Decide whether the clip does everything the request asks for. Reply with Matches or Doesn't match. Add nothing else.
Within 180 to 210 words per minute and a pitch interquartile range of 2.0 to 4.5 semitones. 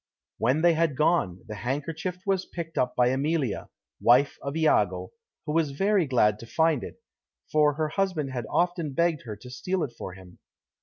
Doesn't match